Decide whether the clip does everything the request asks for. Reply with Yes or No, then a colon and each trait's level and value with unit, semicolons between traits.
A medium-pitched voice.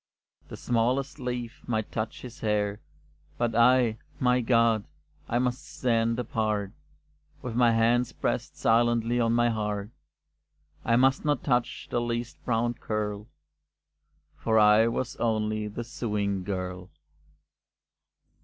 No: low, 115 Hz